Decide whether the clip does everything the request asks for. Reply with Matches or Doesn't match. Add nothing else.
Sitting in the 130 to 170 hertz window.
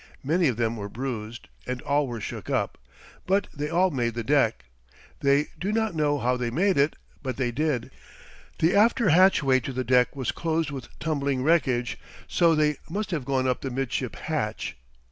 Matches